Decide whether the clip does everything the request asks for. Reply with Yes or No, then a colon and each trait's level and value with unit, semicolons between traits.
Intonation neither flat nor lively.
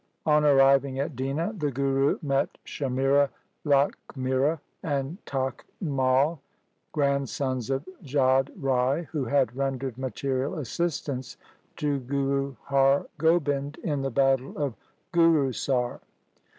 No: narrow, 1.6 semitones